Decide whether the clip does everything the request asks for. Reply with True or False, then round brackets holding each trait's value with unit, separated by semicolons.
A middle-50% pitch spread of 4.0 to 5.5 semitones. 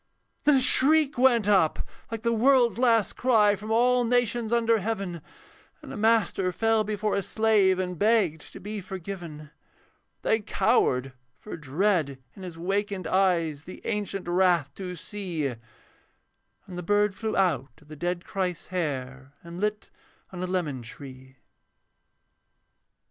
True (4.7 semitones)